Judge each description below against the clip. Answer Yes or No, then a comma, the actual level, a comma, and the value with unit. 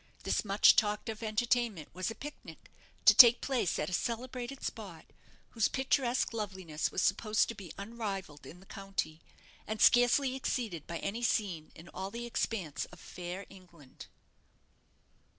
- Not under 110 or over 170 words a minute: Yes, average, 155 wpm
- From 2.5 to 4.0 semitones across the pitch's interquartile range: No, average, 4.7 semitones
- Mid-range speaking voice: No, high, 210 Hz